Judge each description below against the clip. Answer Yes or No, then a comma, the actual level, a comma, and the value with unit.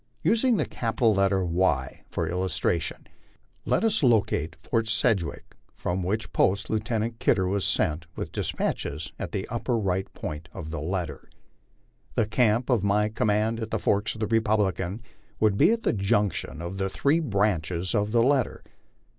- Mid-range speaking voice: No, low, 105 Hz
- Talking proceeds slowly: No, average, 165 wpm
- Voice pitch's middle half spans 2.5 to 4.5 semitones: Yes, average, 3.7 semitones